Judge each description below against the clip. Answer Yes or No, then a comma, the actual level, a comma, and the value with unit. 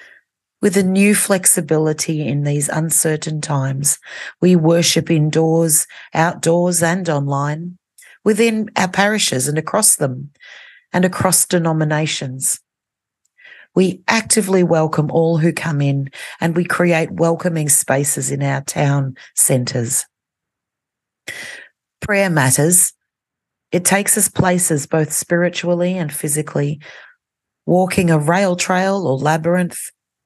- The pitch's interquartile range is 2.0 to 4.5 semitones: Yes, average, 3.4 semitones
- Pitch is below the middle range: No, medium, 165 Hz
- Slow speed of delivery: Yes, slow, 110 wpm